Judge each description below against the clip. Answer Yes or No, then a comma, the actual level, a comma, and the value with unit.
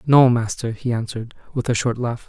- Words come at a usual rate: No, fast, 210 wpm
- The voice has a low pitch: Yes, low, 120 Hz